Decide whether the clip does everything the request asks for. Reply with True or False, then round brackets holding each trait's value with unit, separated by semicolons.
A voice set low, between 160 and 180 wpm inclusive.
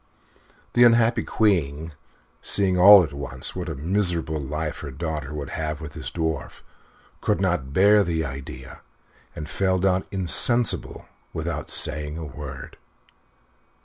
False (80 Hz; 135 wpm)